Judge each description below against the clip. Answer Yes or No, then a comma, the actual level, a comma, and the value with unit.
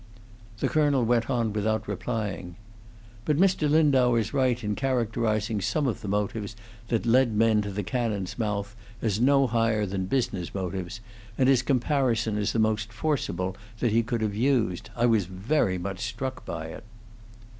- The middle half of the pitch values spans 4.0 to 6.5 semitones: No, average, 3.4 semitones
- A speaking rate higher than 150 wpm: Yes, average, 165 wpm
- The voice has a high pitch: No, low, 110 Hz